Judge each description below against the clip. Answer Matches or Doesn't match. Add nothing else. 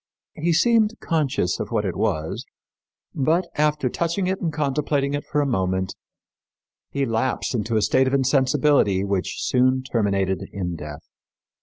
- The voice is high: Doesn't match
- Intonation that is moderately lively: Doesn't match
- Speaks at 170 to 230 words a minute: Doesn't match